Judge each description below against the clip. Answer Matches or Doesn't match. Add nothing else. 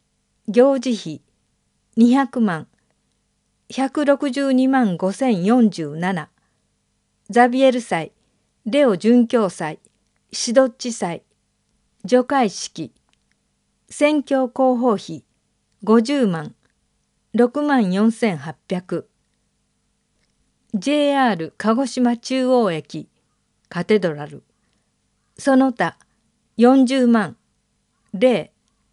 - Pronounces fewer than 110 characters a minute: Matches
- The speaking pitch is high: Matches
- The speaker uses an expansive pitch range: Matches